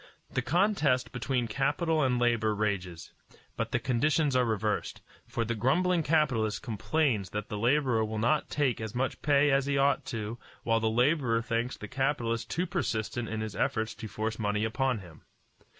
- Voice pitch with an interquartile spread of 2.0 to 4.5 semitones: Yes, average, 4.2 semitones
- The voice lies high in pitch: No, low, 120 Hz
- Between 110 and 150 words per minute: No, average, 175 wpm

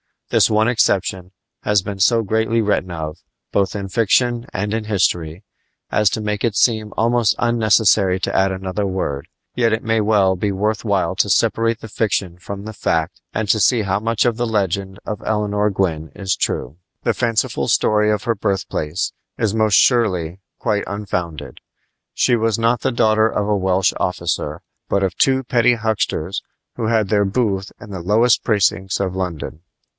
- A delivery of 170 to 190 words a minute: Yes, average, 175 wpm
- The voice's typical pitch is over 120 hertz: No, low, 105 Hz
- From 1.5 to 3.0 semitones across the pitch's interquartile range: Yes, average, 2.7 semitones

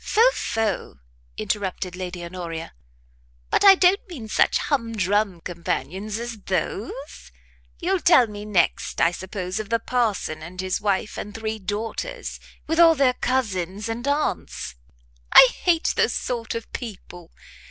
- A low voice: No, high, 215 Hz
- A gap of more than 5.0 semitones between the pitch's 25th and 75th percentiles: Yes, wide, 5.4 semitones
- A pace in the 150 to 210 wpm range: No, average, 140 wpm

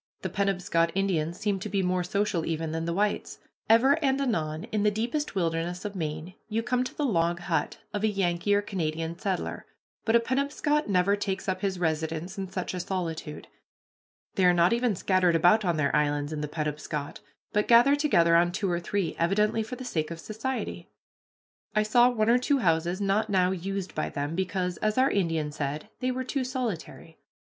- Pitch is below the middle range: No, high, 190 Hz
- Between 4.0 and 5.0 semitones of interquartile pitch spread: Yes, average, 4.5 semitones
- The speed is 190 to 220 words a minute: Yes, average, 195 wpm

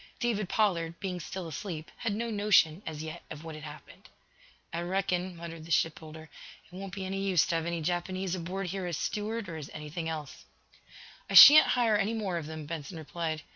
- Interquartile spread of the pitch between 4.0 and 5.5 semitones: No, average, 3.5 semitones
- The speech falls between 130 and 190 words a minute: No, average, 200 wpm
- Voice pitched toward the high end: No, medium, 175 Hz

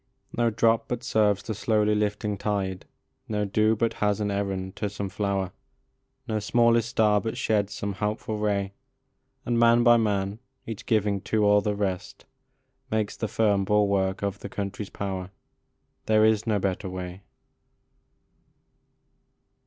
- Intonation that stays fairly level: Yes, narrow, 1.7 semitones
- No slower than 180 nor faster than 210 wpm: No, average, 150 wpm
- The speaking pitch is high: No, low, 105 Hz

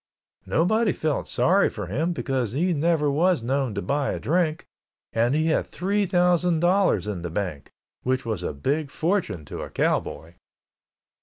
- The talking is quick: No, average, 165 wpm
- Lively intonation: Yes, wide, 7.5 semitones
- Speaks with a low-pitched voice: No, medium, 150 Hz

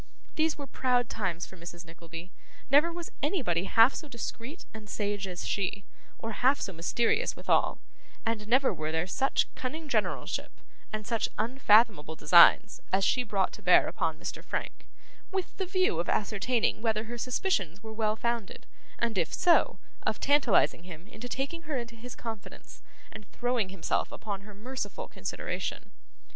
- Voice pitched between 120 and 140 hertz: No, high, 225 Hz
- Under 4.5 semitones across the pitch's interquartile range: No, average, 5.1 semitones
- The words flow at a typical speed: Yes, average, 160 wpm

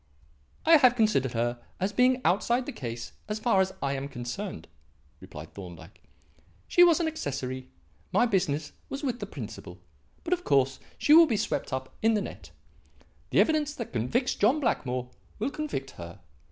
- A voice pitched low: No, high, 195 Hz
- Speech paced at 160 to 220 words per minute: Yes, average, 170 wpm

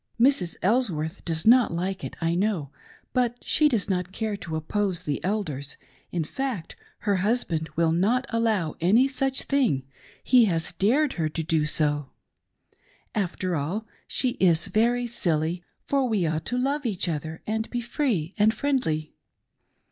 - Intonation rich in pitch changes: Yes, wide, 6.6 semitones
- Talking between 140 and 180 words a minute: Yes, average, 165 wpm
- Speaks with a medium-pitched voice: No, high, 195 Hz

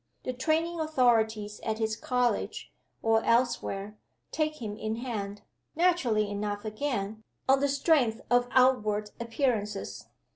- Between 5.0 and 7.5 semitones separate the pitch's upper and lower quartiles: No, average, 3.8 semitones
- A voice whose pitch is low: No, high, 230 Hz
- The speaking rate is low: Yes, slow, 120 wpm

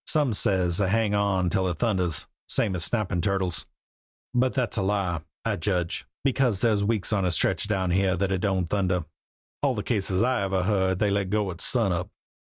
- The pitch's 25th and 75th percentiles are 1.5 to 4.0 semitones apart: Yes, narrow, 2.5 semitones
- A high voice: No, very low, 95 Hz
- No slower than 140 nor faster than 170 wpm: No, average, 200 wpm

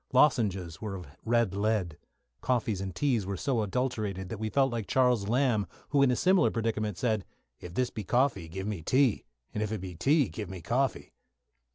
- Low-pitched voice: Yes, low, 110 Hz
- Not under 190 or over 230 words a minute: Yes, average, 195 wpm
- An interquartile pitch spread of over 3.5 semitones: Yes, average, 4.6 semitones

